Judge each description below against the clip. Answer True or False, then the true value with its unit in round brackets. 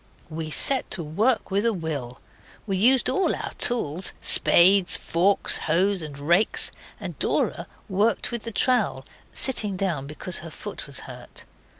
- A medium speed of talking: True (155 wpm)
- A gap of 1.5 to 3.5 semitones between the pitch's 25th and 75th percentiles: False (5.6 semitones)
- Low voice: False (190 Hz)